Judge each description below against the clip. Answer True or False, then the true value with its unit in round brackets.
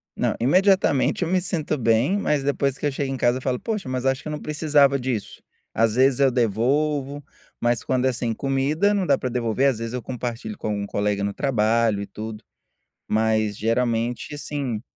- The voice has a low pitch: True (130 Hz)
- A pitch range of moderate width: True (3.9 semitones)